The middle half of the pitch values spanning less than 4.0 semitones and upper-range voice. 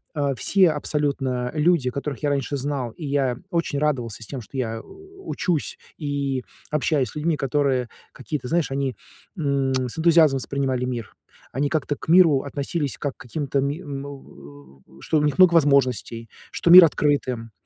No: average, 3.0 semitones; medium, 140 Hz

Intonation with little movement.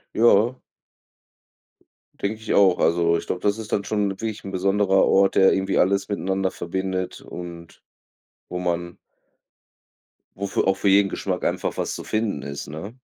Yes: narrow, 2.1 semitones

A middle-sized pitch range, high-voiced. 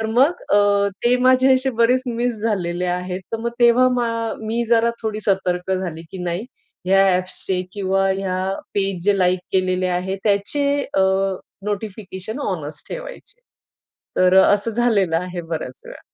Yes: average, 4.2 semitones; high, 200 Hz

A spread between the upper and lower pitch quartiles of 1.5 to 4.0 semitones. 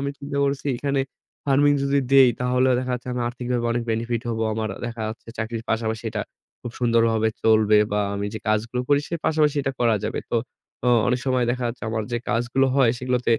Yes: average, 2.9 semitones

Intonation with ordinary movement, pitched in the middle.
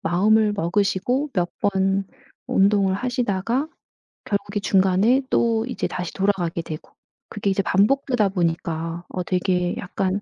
No: average, 3.0 semitones; high, 195 Hz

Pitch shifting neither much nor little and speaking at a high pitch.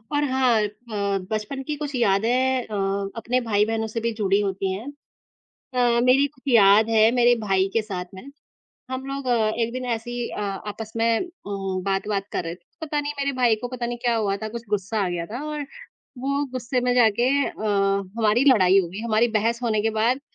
Yes: average, 3.8 semitones; high, 225 Hz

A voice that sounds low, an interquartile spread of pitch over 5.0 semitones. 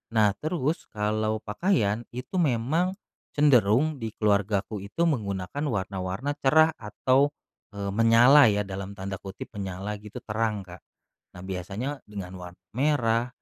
Yes: low, 110 Hz; wide, 5.4 semitones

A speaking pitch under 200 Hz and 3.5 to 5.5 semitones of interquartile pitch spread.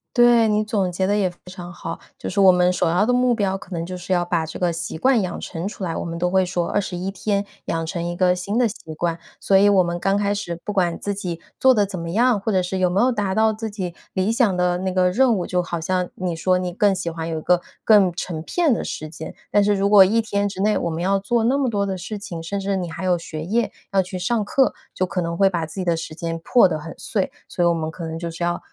No: medium, 185 Hz; average, 2.9 semitones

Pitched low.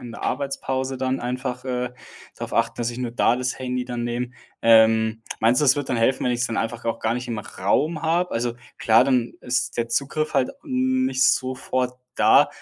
Yes: low, 125 Hz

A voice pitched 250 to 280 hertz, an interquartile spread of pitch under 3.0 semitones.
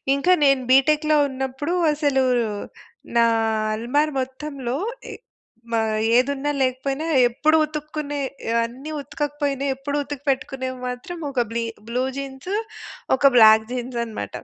Yes: very high, 270 Hz; narrow, 2.4 semitones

